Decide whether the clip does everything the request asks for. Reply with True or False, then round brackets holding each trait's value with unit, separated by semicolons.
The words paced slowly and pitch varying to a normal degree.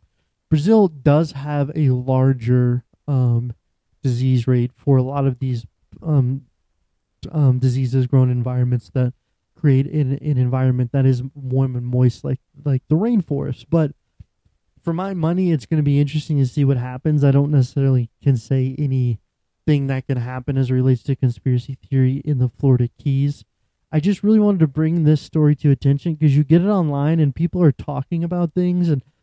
False (180 wpm; 3.0 semitones)